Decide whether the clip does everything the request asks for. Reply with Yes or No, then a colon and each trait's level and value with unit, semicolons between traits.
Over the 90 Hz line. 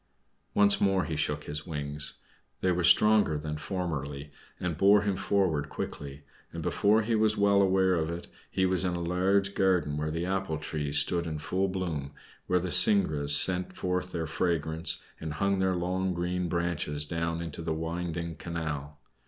No: very low, 85 Hz